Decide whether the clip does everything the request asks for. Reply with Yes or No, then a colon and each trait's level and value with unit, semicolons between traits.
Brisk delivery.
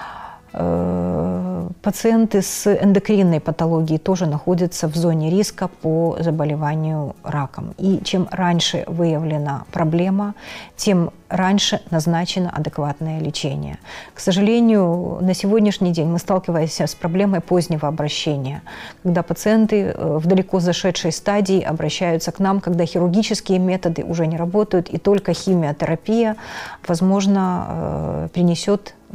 No: average, 110 wpm